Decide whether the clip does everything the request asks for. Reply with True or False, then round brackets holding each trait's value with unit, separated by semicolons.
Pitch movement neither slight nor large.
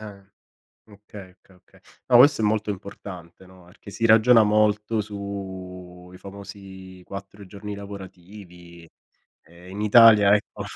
False (2.3 semitones)